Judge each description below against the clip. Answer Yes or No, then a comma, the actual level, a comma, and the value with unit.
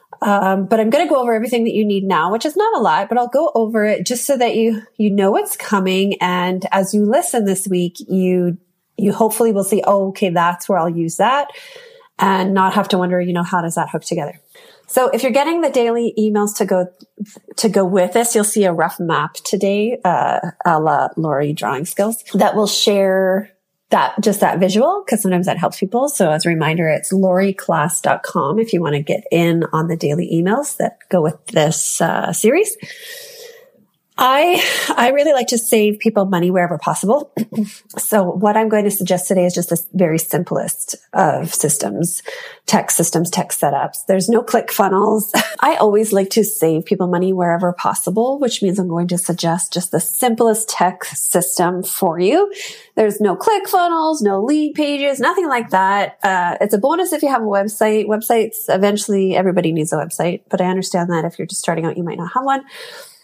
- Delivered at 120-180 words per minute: No, average, 200 wpm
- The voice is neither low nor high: No, high, 200 Hz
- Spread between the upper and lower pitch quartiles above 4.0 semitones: Yes, average, 4.7 semitones